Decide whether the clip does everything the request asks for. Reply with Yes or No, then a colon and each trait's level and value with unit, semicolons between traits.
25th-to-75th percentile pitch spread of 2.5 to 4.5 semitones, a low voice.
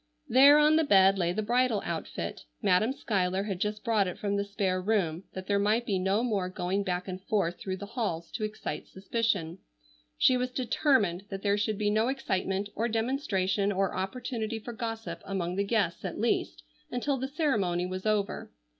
No: average, 3.5 semitones; high, 205 Hz